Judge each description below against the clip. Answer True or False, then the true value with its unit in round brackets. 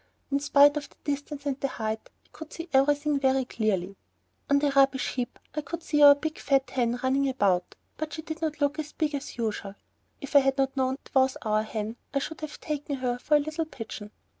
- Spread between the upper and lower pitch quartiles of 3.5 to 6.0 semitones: False (2.9 semitones)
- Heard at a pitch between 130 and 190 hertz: False (275 Hz)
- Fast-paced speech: True (230 wpm)